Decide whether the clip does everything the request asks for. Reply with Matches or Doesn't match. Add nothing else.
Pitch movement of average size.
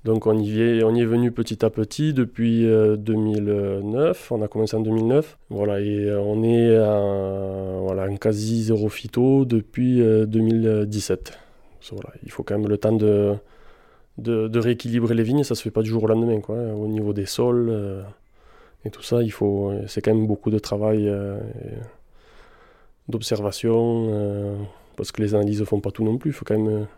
Doesn't match